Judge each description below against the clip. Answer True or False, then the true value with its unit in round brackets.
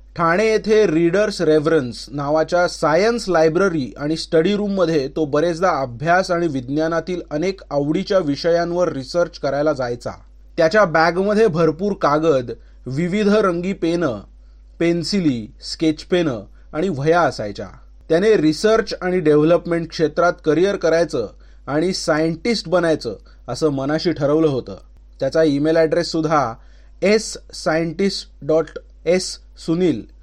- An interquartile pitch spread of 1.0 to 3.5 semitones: True (2.9 semitones)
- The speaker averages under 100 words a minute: False (115 wpm)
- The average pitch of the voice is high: False (165 Hz)